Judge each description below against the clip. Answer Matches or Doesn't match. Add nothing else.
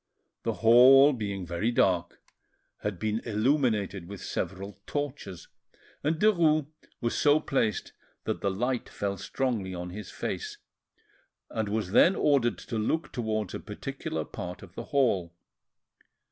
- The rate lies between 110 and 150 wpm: Matches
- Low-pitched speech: Matches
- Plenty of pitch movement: Matches